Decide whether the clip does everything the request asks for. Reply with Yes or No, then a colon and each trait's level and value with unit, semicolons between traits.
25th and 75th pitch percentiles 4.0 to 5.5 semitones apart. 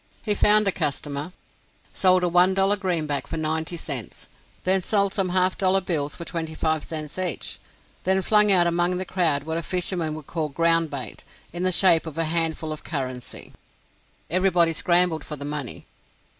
No: average, 3.0 semitones